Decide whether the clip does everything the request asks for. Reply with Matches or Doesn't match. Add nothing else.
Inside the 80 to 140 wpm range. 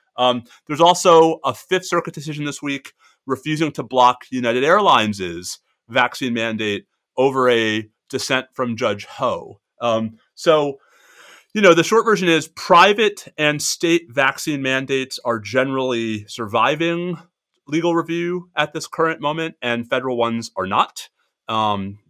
Matches